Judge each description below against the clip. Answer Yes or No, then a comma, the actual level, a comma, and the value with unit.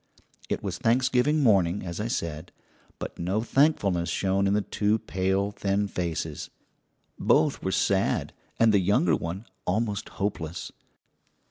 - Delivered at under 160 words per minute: Yes, slow, 135 wpm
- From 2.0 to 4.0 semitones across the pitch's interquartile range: Yes, average, 3.5 semitones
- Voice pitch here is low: Yes, low, 100 Hz